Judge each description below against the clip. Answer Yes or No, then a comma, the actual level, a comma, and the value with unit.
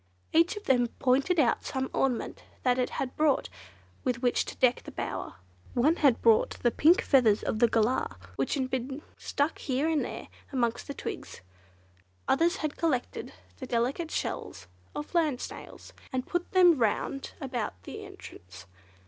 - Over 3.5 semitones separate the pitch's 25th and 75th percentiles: Yes, average, 4.1 semitones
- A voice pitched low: No, very high, 260 Hz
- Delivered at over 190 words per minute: No, average, 165 wpm